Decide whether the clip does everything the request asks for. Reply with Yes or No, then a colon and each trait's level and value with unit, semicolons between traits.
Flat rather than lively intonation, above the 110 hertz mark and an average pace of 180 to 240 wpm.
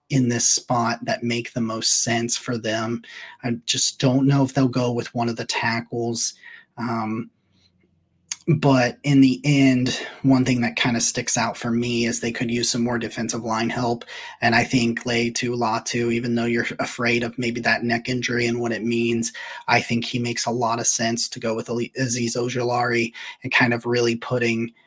Yes: narrow, 0.9 semitones; low, 120 Hz; average, 200 wpm